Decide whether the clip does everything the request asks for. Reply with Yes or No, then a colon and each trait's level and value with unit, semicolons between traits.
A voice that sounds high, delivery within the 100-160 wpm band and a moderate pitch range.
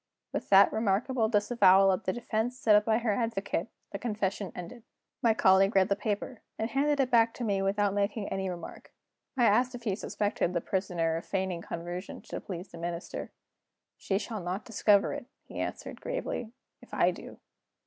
No: high, 205 Hz; average, 185 wpm; average, 3.2 semitones